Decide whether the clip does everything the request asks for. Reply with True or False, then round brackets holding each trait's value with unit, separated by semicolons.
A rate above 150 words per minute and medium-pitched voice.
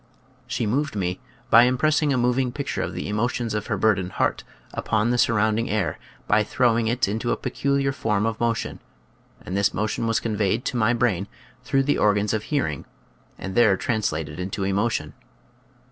False (180 wpm; 110 Hz)